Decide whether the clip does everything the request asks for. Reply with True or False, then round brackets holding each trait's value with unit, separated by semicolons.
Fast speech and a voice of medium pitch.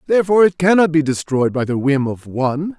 True (215 wpm; 155 Hz)